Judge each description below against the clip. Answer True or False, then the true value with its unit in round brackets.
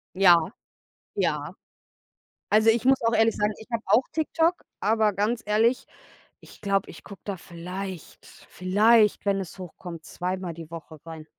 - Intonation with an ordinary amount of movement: True (3.8 semitones)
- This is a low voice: False (200 Hz)